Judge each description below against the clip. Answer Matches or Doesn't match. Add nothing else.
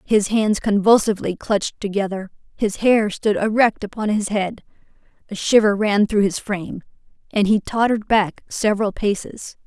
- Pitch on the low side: Doesn't match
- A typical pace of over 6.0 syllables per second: Doesn't match